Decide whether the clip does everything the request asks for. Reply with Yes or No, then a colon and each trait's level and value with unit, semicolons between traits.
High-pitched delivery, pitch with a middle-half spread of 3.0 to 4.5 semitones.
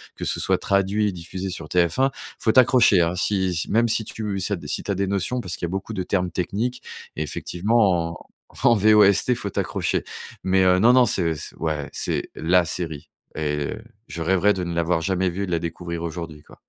No: very low, 95 Hz; average, 3.4 semitones